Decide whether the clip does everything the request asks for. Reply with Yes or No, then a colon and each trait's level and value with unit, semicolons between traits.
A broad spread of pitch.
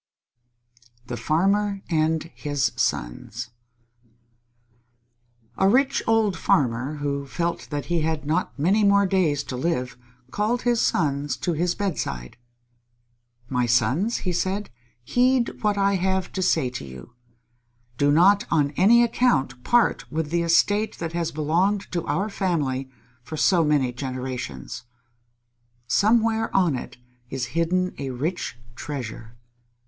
Yes: wide, 6.5 semitones